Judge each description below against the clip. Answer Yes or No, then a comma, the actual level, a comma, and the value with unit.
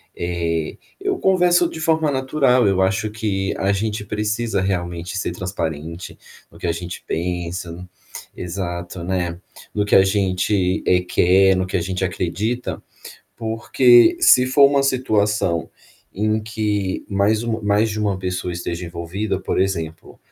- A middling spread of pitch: Yes, average, 3.7 semitones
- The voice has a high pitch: No, very low, 95 Hz